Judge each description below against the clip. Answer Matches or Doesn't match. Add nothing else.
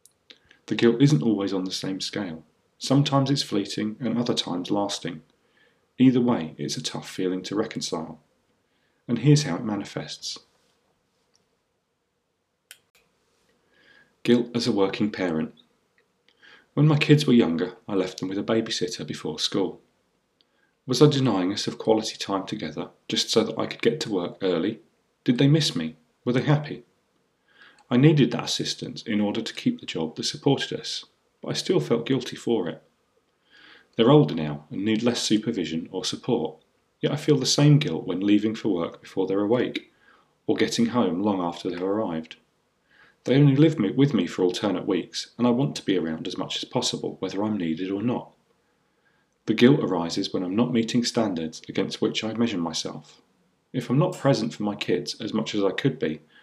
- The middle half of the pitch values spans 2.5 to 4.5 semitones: Doesn't match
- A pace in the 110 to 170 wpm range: Doesn't match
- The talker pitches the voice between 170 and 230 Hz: Doesn't match